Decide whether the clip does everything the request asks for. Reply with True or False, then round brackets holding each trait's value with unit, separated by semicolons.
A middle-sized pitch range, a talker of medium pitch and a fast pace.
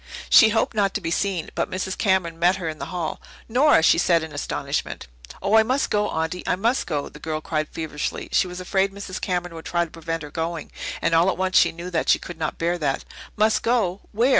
True (3.4 semitones; 175 Hz; 240 wpm)